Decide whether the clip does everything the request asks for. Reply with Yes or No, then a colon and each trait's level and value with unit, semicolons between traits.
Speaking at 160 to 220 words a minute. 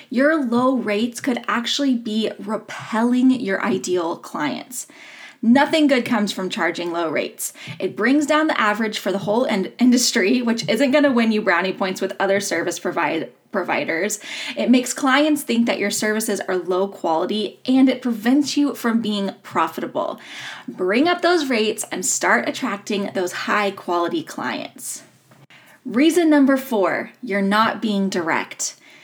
No: average, 150 wpm